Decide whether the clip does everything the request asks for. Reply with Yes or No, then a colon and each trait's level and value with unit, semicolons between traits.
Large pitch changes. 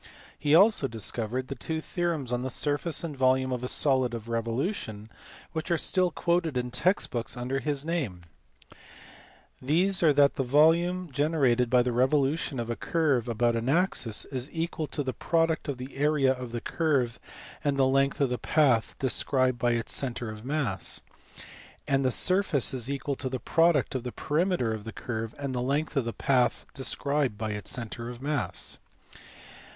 No: average, 4.0 semitones